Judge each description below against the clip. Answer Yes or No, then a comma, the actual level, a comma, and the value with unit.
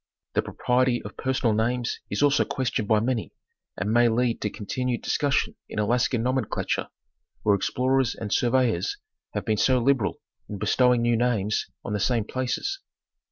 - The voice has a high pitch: No, low, 120 Hz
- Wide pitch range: No, average, 2.9 semitones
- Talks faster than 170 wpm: No, average, 160 wpm